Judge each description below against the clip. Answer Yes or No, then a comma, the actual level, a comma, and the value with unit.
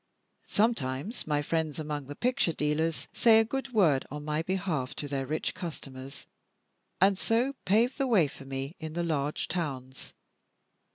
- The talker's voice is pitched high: No, medium, 160 Hz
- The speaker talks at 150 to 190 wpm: Yes, average, 160 wpm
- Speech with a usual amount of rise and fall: No, wide, 6.0 semitones